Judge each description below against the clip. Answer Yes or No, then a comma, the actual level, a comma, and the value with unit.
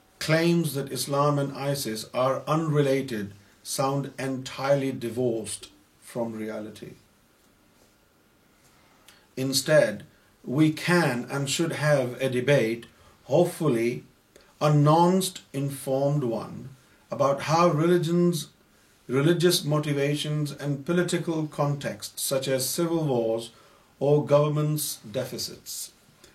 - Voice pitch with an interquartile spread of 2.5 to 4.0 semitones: Yes, average, 3.1 semitones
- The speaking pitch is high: No, medium, 140 Hz